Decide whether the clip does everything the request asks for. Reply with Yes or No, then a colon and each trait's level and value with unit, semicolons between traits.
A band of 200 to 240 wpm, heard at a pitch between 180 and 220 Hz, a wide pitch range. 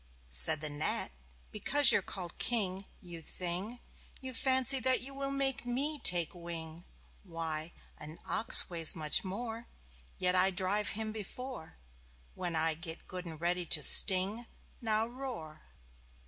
No: average, 145 wpm; medium, 185 Hz; wide, 6.5 semitones